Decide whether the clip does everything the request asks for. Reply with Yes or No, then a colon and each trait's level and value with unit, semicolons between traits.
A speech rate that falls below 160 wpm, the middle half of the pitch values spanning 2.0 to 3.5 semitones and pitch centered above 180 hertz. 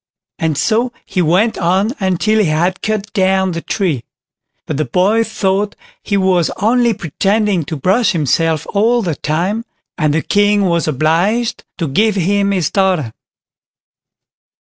No: average, 150 wpm; average, 4.2 semitones; high, 190 Hz